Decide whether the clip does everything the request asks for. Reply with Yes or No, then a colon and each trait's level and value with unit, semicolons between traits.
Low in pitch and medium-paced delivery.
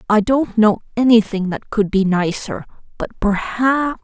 No: high, 220 Hz; average, 150 wpm